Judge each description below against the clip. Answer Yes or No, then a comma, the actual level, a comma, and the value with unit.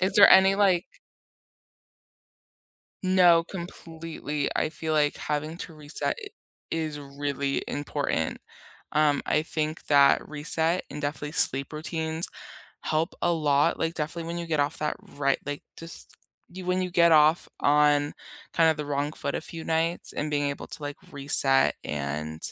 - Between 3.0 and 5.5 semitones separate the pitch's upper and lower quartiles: No, narrow, 2.5 semitones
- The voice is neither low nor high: Yes, medium, 155 Hz